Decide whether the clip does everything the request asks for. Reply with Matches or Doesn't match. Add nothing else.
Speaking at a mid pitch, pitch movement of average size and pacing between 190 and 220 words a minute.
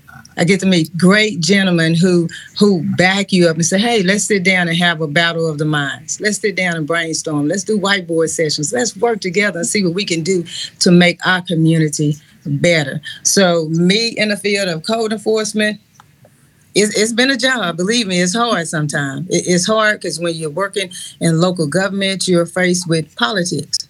Matches